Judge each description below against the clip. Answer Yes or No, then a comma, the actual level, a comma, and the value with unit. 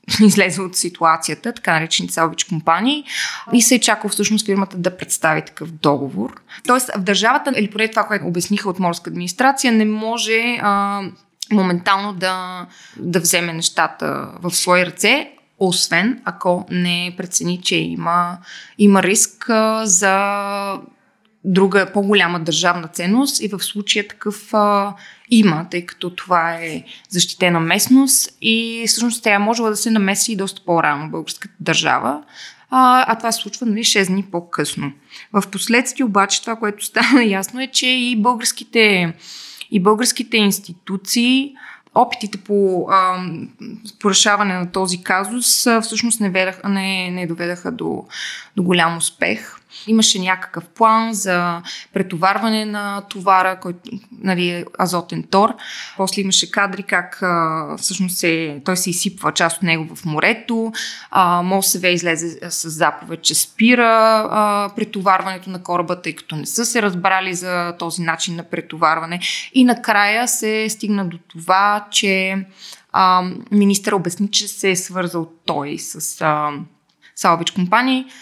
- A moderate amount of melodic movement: Yes, average, 3.7 semitones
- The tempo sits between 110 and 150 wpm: Yes, average, 140 wpm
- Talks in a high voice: Yes, high, 195 Hz